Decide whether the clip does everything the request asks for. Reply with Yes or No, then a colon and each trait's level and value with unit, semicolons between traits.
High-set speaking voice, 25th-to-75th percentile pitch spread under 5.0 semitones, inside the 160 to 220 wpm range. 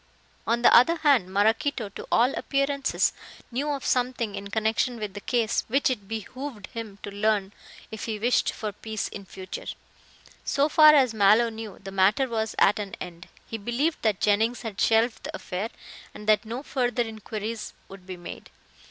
Yes: high, 225 Hz; average, 3.5 semitones; average, 180 wpm